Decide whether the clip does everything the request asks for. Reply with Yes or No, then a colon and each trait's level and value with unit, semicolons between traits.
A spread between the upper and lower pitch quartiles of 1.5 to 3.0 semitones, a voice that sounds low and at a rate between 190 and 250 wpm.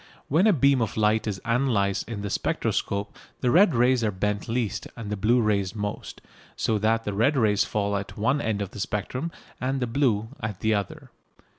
No: average, 3.4 semitones; low, 110 Hz; average, 200 wpm